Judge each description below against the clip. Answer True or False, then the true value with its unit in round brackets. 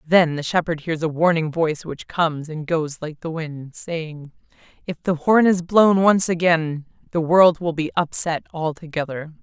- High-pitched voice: False (160 Hz)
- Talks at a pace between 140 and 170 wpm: False (180 wpm)